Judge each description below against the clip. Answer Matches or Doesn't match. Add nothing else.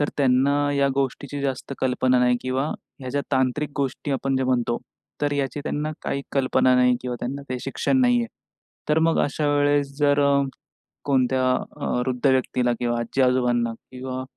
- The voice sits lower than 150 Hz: Matches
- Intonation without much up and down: Matches